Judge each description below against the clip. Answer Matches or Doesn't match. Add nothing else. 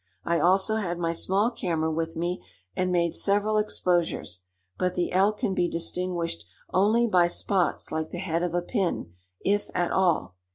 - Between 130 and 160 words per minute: Doesn't match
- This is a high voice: Doesn't match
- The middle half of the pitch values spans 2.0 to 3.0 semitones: Matches